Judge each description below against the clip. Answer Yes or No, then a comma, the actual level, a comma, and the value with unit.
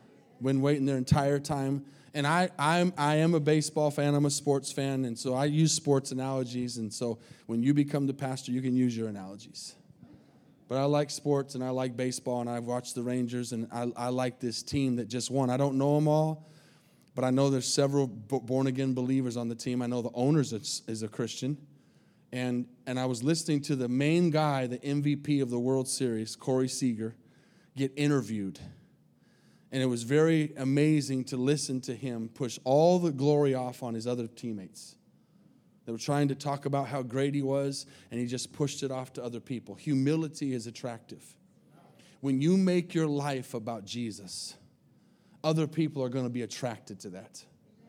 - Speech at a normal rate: Yes, average, 195 wpm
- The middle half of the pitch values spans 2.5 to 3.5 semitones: Yes, average, 2.8 semitones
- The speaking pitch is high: No, low, 135 Hz